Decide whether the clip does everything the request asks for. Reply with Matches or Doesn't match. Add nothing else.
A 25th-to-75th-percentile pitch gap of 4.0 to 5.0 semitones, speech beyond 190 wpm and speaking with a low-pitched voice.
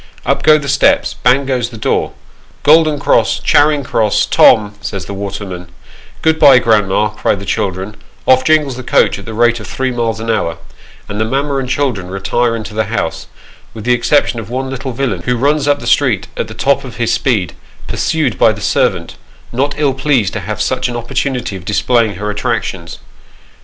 Matches